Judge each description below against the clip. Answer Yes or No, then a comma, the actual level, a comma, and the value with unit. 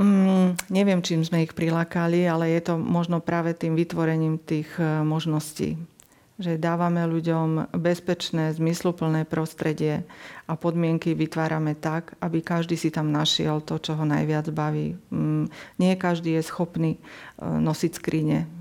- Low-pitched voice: No, medium, 165 Hz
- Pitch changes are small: Yes, narrow, 1.5 semitones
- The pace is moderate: Yes, average, 140 wpm